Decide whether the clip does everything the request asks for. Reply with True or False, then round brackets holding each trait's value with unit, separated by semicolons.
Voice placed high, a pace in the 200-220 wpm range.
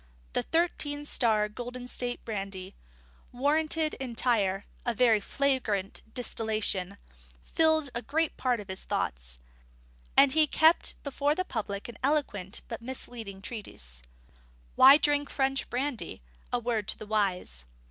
False (240 Hz; 135 wpm)